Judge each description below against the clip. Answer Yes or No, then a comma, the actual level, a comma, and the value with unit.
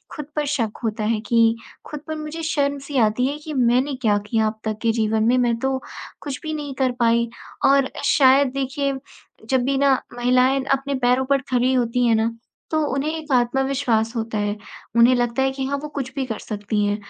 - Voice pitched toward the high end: Yes, very high, 255 Hz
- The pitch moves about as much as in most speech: Yes, average, 3.2 semitones